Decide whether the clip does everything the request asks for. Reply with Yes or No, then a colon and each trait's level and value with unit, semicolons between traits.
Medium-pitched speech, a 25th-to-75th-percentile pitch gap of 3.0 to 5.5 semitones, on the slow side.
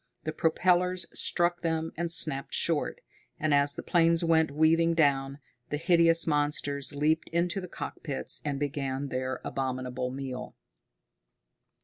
Yes: medium, 155 Hz; average, 3.3 semitones; slow, 130 wpm